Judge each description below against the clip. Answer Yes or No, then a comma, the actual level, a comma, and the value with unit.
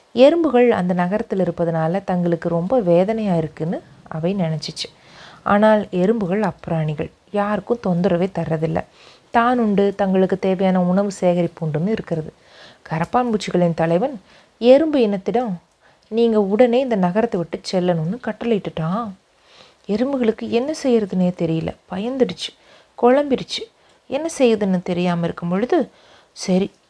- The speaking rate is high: No, average, 105 wpm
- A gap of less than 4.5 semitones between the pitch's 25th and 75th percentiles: No, average, 4.8 semitones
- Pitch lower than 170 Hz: No, high, 195 Hz